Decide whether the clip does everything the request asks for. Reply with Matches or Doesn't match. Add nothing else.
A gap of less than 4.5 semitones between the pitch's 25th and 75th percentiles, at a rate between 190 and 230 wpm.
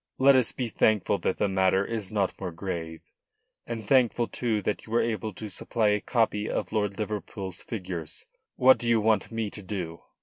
Matches